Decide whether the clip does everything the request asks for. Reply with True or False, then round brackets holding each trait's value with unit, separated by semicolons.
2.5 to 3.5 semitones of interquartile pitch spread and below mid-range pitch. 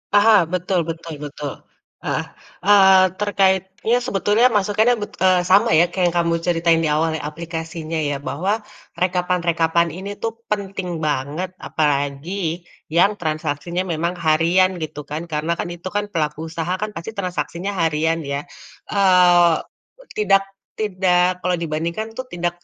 False (2.9 semitones; 175 Hz)